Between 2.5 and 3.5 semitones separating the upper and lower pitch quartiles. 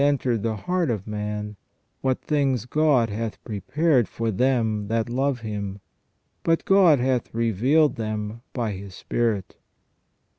No: average, 4.3 semitones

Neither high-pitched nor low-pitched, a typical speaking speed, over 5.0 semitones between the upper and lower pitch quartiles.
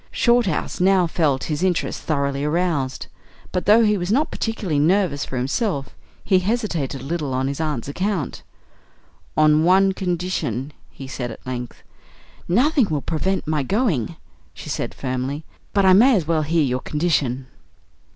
Yes: medium, 160 Hz; average, 155 wpm; wide, 5.4 semitones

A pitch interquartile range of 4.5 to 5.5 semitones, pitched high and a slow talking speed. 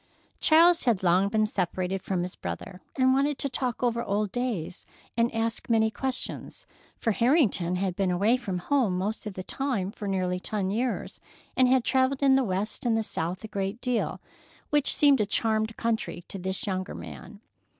No: average, 5.1 semitones; high, 220 Hz; average, 185 wpm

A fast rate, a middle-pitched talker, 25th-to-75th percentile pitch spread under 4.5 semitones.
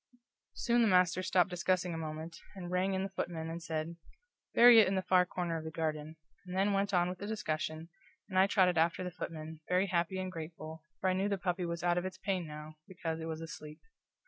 Yes: fast, 230 wpm; medium, 175 Hz; narrow, 2.5 semitones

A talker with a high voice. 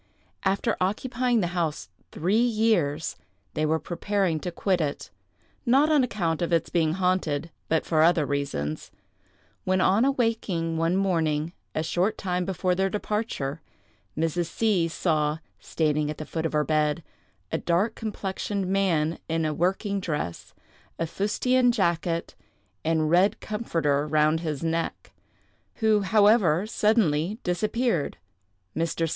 No: medium, 175 Hz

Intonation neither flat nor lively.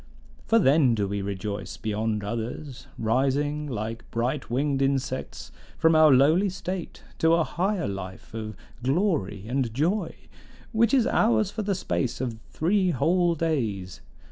No: wide, 7.3 semitones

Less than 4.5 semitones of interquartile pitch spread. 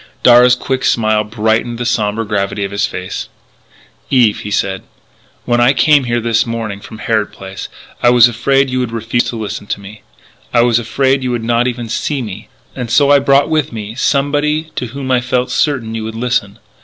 Yes: average, 2.8 semitones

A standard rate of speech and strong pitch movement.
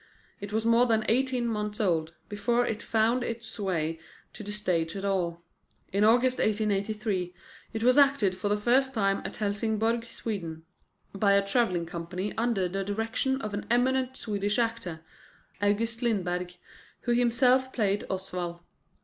No: average, 150 wpm; average, 3.4 semitones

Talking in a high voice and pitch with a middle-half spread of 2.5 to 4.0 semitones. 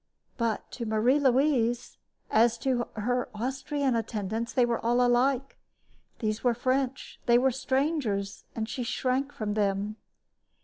Yes: high, 240 Hz; average, 3.0 semitones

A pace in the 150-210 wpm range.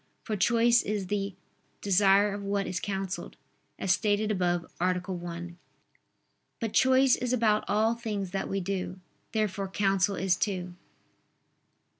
No: slow, 135 wpm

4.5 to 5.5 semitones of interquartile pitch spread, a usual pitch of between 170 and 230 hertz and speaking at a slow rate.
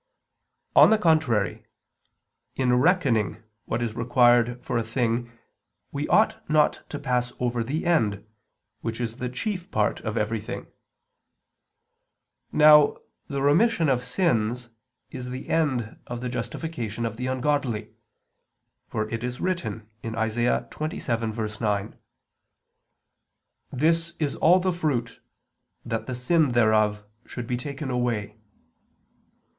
No: average, 4.9 semitones; low, 125 Hz; slow, 120 wpm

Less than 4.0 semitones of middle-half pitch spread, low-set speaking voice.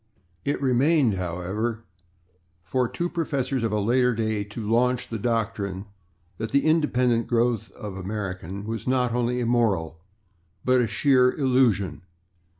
Yes: average, 3.5 semitones; low, 115 Hz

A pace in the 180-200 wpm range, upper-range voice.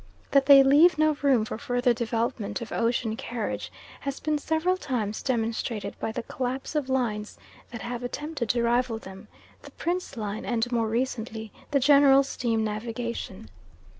No: average, 160 wpm; high, 240 Hz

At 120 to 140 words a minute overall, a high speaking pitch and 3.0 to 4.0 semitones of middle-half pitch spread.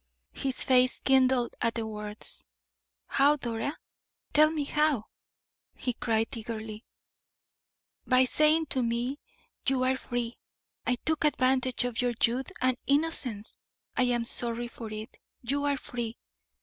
No: slow, 135 wpm; very high, 250 Hz; narrow, 2.6 semitones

